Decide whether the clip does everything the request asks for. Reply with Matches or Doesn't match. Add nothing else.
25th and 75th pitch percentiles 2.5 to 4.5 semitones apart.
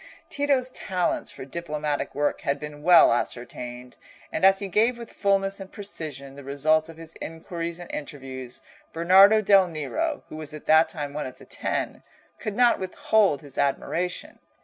Doesn't match